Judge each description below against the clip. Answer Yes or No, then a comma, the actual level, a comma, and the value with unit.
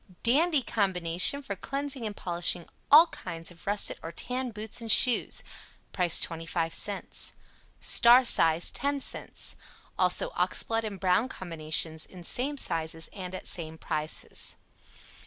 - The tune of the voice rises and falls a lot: Yes, wide, 6.8 semitones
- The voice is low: No, high, 195 Hz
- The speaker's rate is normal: No, slow, 125 wpm